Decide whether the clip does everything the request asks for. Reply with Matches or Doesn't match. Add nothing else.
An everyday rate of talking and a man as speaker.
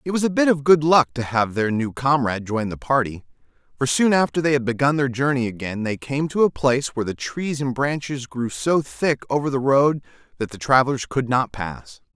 Doesn't match